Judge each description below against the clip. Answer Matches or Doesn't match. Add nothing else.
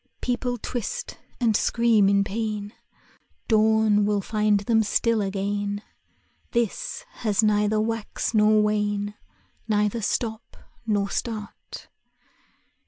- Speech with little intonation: Matches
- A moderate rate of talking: Doesn't match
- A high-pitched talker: Matches